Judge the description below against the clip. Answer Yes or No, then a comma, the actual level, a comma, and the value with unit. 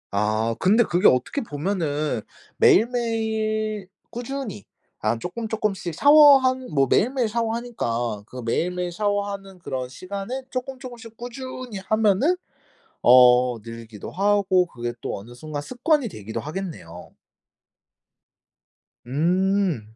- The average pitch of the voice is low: No, high, 195 Hz